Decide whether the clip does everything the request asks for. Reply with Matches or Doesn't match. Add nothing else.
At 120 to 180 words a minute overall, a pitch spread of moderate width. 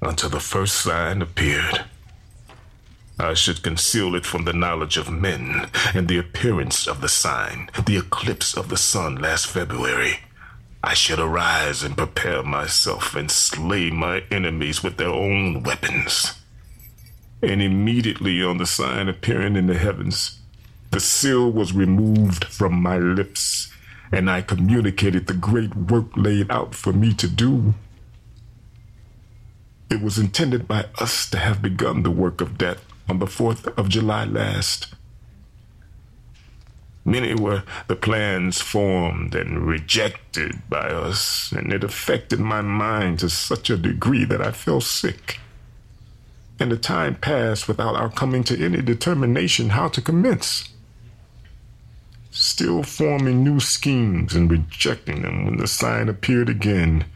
Matches